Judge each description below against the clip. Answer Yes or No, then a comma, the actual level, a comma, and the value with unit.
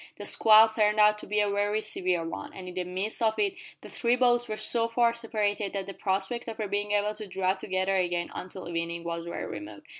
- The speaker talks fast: Yes, fast, 235 wpm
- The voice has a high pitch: Yes, high, 205 Hz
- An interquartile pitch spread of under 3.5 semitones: Yes, average, 2.8 semitones